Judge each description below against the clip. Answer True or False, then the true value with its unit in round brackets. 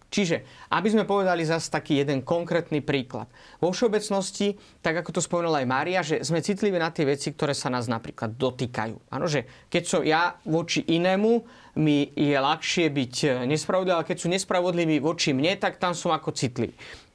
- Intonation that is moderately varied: True (4.1 semitones)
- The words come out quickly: True (180 wpm)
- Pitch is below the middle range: False (165 Hz)